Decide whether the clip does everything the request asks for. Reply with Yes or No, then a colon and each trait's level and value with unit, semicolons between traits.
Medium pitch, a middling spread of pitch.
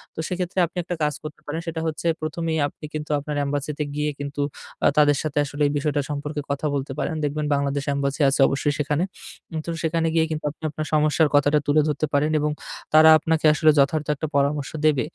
No: medium, 150 Hz; narrow, 1.5 semitones